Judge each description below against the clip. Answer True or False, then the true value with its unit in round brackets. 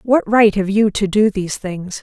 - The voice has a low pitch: False (205 Hz)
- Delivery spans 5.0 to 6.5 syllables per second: False (4.7 syllables/s)